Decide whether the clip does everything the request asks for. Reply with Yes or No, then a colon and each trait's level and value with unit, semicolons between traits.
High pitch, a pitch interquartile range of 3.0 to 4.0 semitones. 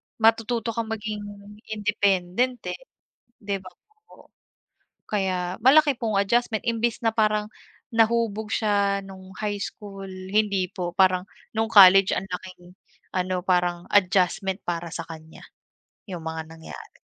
Yes: high, 200 Hz; average, 3.3 semitones